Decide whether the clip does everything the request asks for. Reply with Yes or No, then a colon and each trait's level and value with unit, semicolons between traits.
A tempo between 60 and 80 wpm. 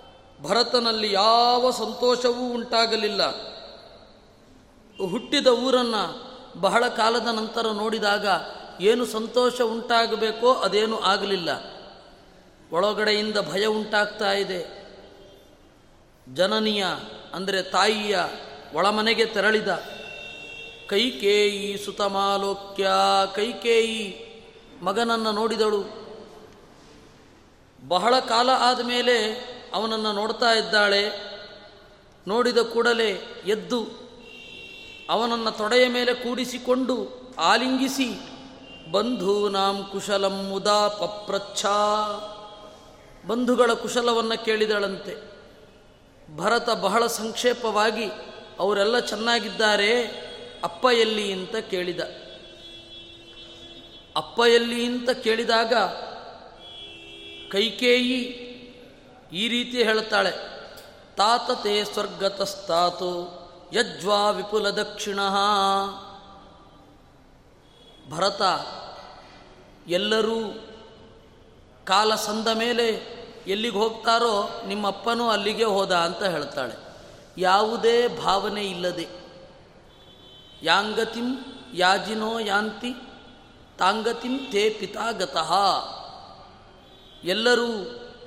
Yes: slow, 65 wpm